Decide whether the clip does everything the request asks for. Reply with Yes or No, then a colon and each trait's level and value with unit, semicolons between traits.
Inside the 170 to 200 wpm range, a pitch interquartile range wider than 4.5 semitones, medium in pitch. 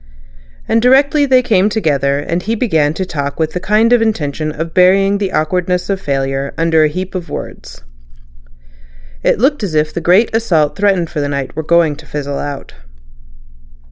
Yes: average, 175 wpm; wide, 5.4 semitones; medium, 170 Hz